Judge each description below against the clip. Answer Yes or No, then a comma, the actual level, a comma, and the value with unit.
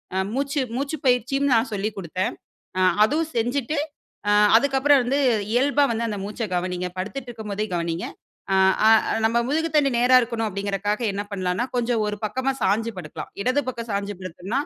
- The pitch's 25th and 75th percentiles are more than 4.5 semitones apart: Yes, average, 5.2 semitones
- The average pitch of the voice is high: Yes, high, 230 Hz